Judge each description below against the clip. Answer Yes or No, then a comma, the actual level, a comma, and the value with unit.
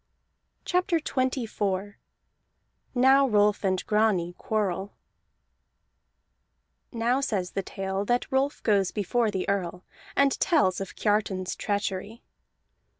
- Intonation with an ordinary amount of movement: Yes, average, 4.3 semitones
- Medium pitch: No, high, 210 Hz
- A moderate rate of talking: No, slow, 100 wpm